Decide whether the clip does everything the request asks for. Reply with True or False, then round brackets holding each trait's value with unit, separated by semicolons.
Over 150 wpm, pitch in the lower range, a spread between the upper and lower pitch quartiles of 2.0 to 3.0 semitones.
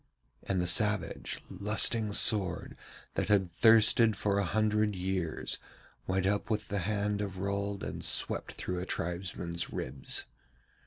False (140 wpm; 100 Hz; 2.4 semitones)